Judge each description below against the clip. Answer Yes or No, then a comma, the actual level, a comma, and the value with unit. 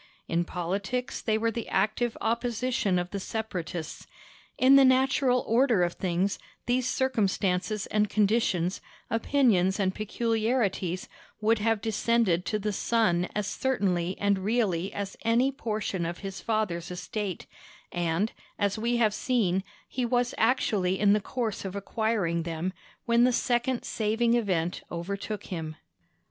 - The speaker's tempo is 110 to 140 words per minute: Yes, slow, 135 wpm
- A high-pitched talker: Yes, high, 210 Hz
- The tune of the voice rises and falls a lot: No, average, 4.2 semitones